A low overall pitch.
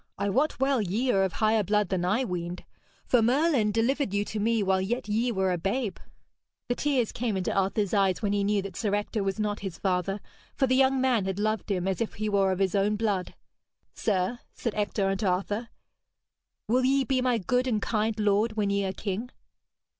No: high, 210 Hz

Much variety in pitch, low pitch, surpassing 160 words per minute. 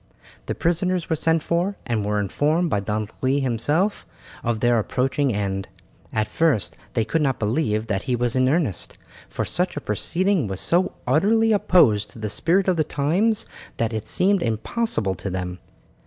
Yes: wide, 8.1 semitones; low, 130 Hz; average, 175 wpm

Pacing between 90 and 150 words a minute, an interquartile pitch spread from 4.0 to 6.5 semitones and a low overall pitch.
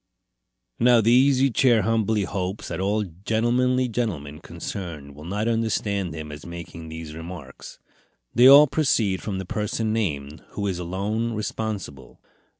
Yes: average, 145 wpm; average, 5.2 semitones; low, 100 Hz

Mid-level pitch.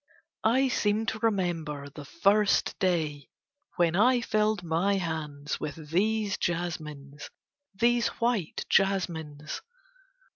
Yes: medium, 175 Hz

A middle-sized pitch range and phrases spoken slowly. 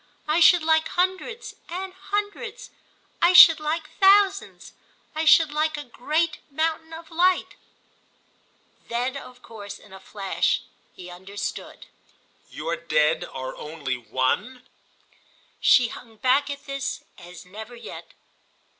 No: wide, 8.1 semitones; slow, 120 wpm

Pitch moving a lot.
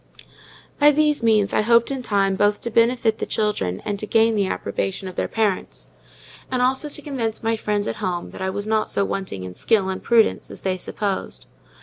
No: average, 3.1 semitones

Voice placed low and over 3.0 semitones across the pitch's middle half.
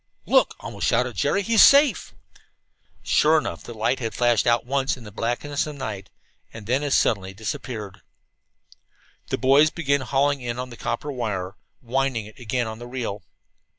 Yes: low, 120 Hz; average, 4.0 semitones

